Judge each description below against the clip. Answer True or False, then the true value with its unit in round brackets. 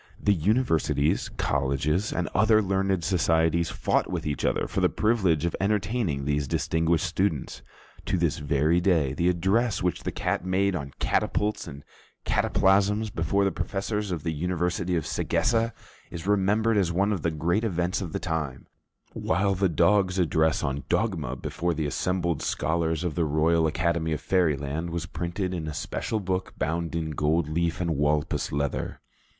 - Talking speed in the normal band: True (165 wpm)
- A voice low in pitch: True (85 Hz)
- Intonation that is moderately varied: True (3.7 semitones)